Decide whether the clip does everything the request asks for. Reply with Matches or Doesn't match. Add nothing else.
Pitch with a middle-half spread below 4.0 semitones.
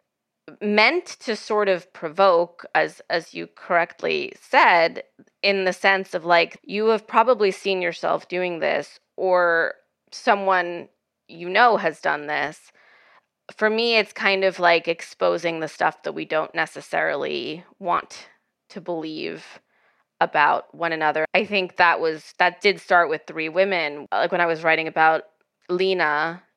Matches